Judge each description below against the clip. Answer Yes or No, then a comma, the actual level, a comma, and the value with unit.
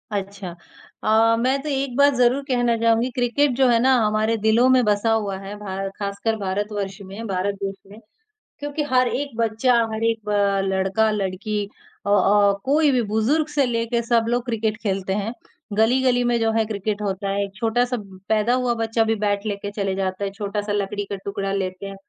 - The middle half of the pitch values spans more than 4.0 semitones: No, average, 3.1 semitones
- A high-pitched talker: Yes, high, 220 Hz